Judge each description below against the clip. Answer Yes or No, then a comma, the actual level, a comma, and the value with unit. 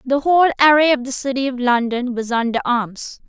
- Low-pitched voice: No, very high, 260 Hz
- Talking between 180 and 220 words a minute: Yes, average, 200 wpm